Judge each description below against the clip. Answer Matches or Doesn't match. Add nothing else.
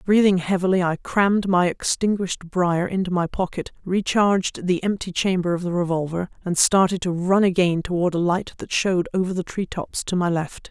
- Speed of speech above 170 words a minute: Matches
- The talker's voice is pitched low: Doesn't match